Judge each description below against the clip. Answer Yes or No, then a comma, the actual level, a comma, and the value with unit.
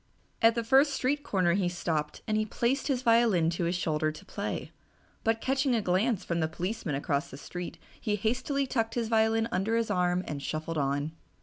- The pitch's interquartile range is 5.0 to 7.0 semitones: Yes, wide, 5.5 semitones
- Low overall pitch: No, high, 210 Hz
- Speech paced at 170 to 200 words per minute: Yes, average, 195 wpm